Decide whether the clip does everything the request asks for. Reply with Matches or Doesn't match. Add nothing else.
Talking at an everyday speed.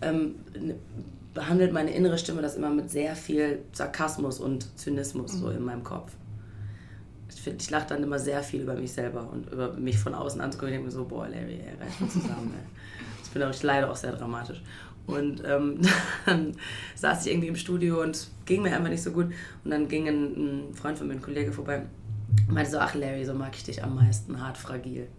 Doesn't match